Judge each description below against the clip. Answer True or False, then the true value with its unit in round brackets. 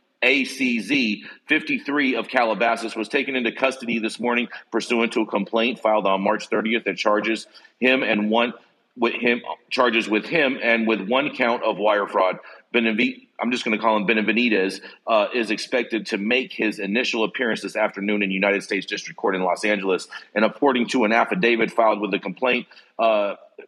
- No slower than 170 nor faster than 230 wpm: True (180 wpm)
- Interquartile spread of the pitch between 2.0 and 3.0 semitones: True (2.7 semitones)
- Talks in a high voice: False (115 Hz)